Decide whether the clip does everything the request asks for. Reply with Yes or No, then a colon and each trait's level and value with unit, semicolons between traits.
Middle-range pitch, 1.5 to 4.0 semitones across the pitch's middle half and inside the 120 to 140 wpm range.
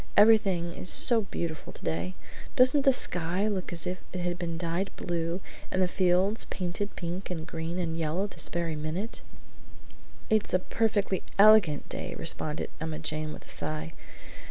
No: medium, 175 Hz; average, 3.4 semitones; average, 160 wpm